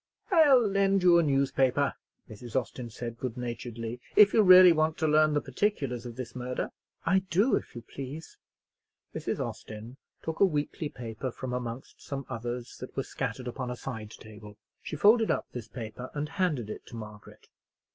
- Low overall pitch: Yes, low, 130 Hz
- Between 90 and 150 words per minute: No, average, 175 wpm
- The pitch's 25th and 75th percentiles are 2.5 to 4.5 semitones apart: No, average, 5.3 semitones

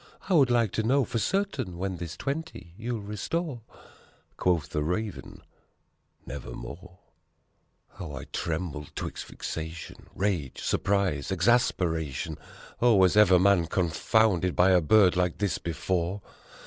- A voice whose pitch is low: Yes, very low, 95 Hz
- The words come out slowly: Yes, slow, 130 wpm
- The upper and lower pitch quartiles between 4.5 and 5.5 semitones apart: Yes, average, 4.8 semitones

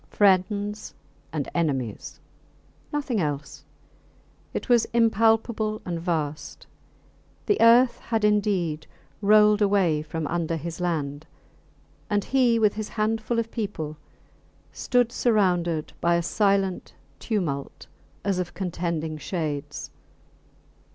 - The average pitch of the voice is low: No, high, 190 Hz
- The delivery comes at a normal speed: No, slow, 105 wpm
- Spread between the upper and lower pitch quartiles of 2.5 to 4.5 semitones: No, average, 5.0 semitones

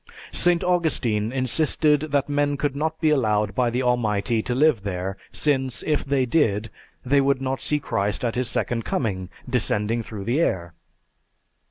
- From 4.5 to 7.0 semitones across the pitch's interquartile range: Yes, average, 5.1 semitones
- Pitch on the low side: Yes, low, 125 Hz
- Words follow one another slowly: No, average, 165 wpm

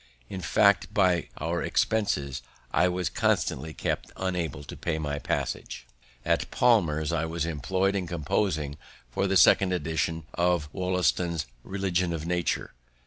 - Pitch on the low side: Yes, very low, 85 Hz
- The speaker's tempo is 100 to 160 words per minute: Yes, average, 140 wpm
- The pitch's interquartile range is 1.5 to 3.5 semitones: Yes, average, 2.9 semitones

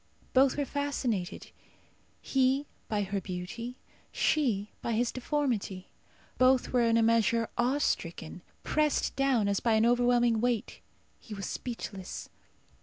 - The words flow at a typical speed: No, slow, 130 wpm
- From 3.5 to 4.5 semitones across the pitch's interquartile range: Yes, average, 3.8 semitones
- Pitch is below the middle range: No, high, 235 Hz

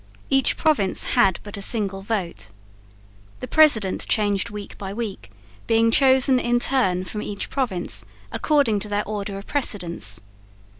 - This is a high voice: Yes, high, 210 Hz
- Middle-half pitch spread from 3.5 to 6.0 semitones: Yes, average, 3.8 semitones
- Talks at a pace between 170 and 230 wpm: No, average, 145 wpm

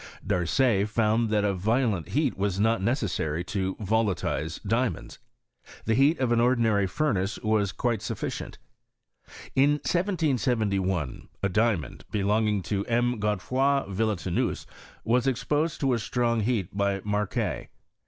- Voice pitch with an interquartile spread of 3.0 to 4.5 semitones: Yes, average, 3.8 semitones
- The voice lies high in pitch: No, low, 110 Hz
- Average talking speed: No, slow, 125 wpm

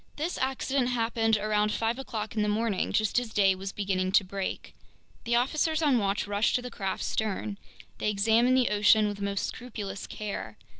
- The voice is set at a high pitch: Yes, high, 215 Hz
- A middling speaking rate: Yes, average, 190 wpm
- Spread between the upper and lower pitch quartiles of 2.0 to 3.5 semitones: Yes, average, 3.2 semitones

